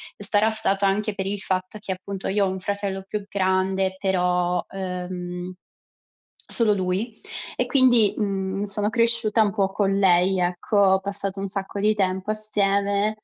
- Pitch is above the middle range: Yes, high, 195 Hz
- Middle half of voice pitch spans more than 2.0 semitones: No, narrow, 1.7 semitones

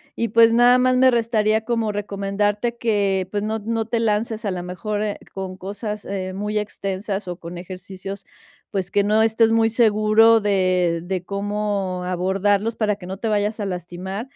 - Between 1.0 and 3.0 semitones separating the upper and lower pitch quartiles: Yes, narrow, 2.6 semitones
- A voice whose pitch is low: No, high, 205 Hz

